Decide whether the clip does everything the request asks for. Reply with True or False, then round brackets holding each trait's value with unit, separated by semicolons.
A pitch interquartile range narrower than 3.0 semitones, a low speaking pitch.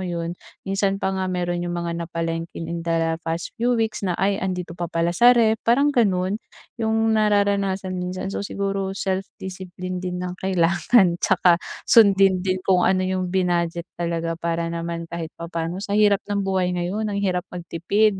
False (2.4 semitones; 185 Hz)